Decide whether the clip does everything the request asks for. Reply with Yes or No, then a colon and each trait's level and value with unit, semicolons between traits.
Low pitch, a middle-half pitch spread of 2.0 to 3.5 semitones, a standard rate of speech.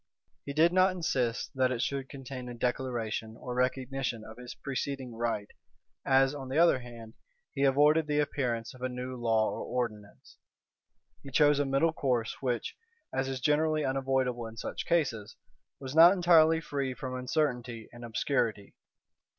Yes: low, 130 Hz; average, 3.1 semitones; average, 160 wpm